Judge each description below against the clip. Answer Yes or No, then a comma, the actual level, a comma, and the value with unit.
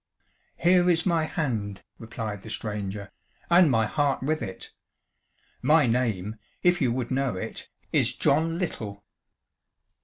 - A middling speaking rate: No, slow, 130 wpm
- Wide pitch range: Yes, wide, 7.2 semitones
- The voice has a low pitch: Yes, low, 125 Hz